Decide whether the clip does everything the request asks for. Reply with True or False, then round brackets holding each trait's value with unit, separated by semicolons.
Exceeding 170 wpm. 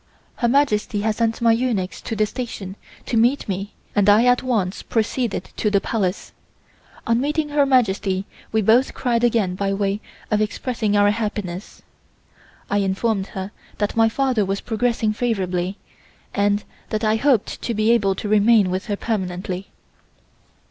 False (160 wpm)